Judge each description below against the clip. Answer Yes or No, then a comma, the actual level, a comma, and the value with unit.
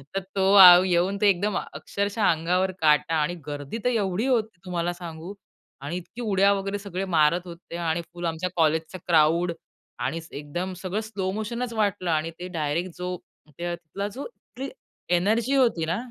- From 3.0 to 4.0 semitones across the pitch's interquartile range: Yes, average, 3.3 semitones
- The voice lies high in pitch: No, medium, 180 Hz